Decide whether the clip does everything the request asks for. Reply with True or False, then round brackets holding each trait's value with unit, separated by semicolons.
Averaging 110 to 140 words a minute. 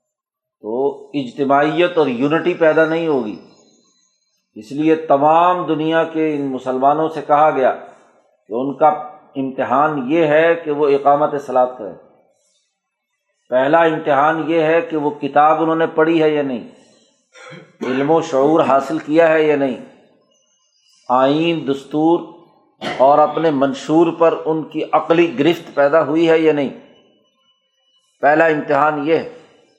True (135 wpm)